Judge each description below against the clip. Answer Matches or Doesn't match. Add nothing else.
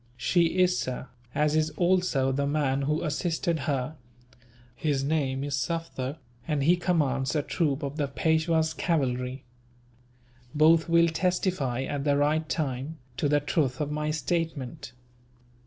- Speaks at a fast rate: Doesn't match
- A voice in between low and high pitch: Matches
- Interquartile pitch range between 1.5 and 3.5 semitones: Matches